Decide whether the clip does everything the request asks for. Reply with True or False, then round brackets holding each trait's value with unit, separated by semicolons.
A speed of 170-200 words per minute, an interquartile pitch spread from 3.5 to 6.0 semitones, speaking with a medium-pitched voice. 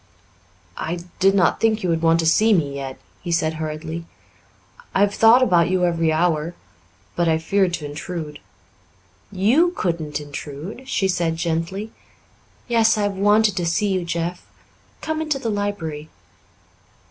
False (155 wpm; 4.0 semitones; 175 Hz)